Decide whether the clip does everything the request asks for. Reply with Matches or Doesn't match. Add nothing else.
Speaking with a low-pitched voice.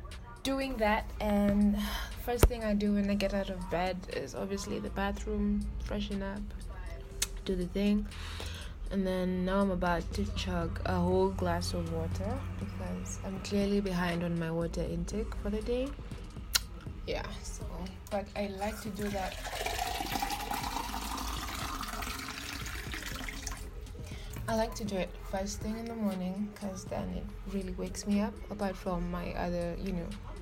Doesn't match